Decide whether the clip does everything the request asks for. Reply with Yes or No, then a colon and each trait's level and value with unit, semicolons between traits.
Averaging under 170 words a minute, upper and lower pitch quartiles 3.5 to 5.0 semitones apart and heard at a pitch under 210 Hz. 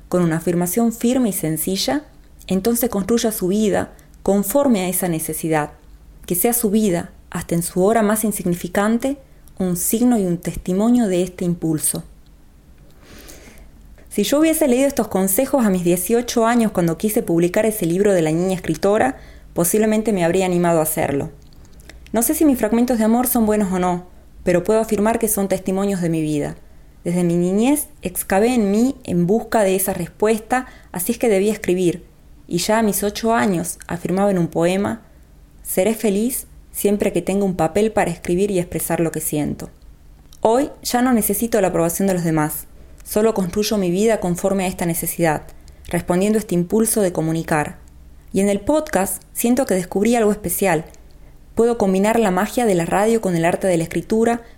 No: average, 180 wpm; average, 4.5 semitones; high, 190 Hz